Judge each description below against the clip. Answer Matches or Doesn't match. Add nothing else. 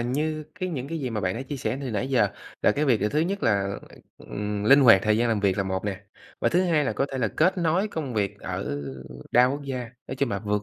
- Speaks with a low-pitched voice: Matches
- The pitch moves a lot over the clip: Matches